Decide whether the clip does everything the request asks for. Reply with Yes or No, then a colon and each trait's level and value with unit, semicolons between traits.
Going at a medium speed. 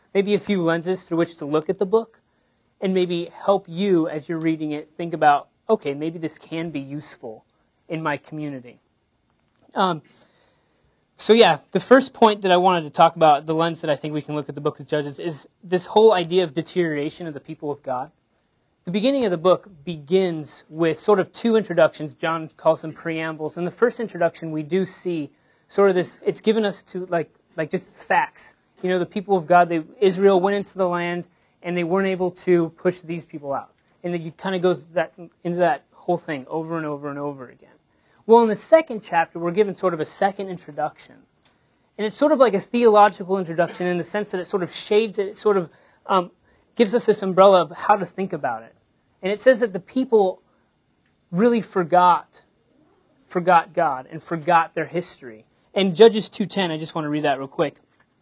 No: fast, 210 wpm